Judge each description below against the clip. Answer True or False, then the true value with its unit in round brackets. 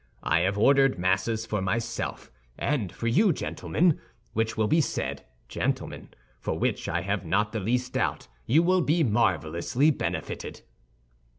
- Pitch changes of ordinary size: False (6.3 semitones)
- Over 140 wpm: True (150 wpm)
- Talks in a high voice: False (115 Hz)